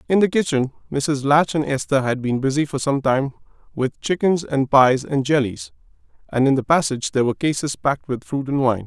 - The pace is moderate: No, fast, 210 wpm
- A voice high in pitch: No, medium, 140 Hz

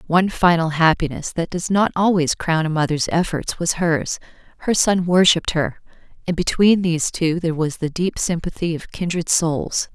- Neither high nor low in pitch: Yes, medium, 170 Hz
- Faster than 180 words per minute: No, average, 170 wpm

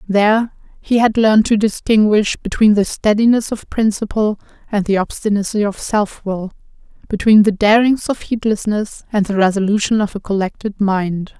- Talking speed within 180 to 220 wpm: No, average, 155 wpm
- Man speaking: No, female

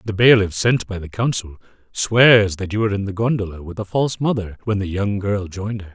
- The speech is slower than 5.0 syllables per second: No, 5.8 syllables/s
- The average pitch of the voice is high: No, low, 100 Hz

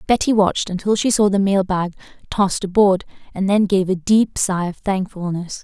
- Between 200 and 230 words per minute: No, average, 190 wpm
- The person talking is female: Yes, female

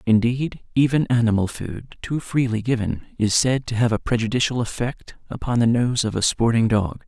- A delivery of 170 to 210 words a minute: Yes, average, 180 wpm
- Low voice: Yes, low, 115 Hz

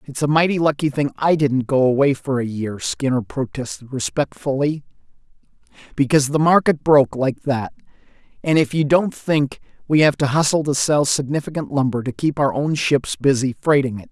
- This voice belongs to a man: Yes, male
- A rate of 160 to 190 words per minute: Yes, average, 170 wpm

